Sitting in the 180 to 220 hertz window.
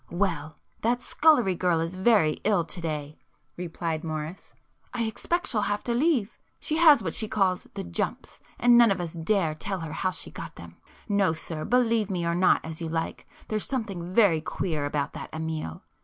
Yes: medium, 185 Hz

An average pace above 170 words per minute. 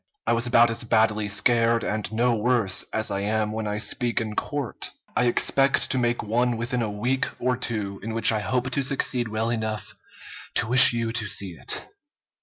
Yes: average, 200 wpm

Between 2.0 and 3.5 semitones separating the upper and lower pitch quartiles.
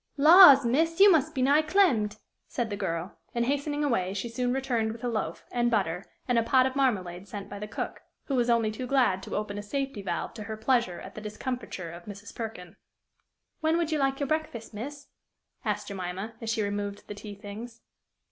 No: average, 4.9 semitones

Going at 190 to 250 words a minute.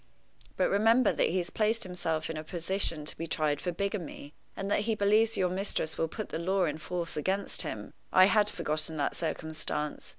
Yes: average, 200 wpm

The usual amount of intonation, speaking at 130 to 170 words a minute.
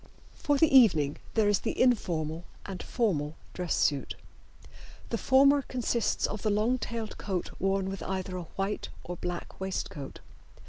Yes: average, 4.8 semitones; average, 150 wpm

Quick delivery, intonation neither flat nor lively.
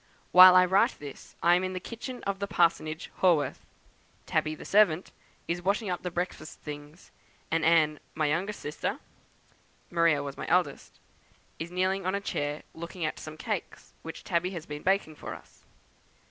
No: average, 175 wpm; average, 3.2 semitones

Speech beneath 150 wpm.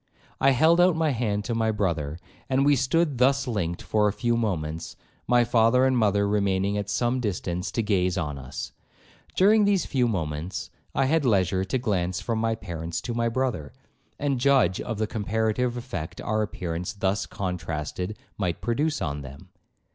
No: average, 175 wpm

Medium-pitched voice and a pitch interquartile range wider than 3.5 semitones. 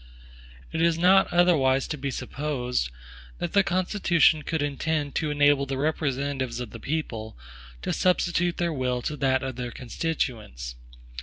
Yes: medium, 145 Hz; average, 4.2 semitones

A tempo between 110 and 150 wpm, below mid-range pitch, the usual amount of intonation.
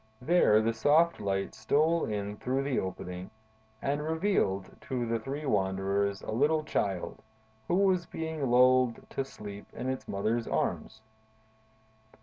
No: slow, 135 wpm; low, 120 Hz; wide, 6.8 semitones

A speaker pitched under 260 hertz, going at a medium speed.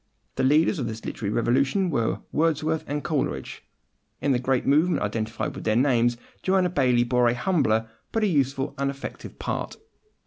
Yes: low, 135 Hz; average, 170 wpm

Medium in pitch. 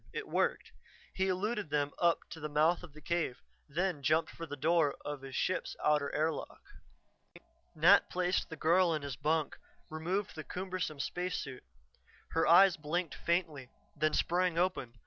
Yes: medium, 160 Hz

